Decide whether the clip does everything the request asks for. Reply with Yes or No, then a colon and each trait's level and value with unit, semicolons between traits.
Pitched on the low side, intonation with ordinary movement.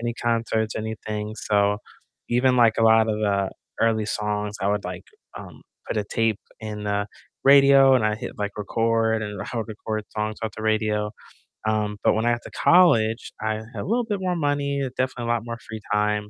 No: low, 110 Hz; narrow, 2.0 semitones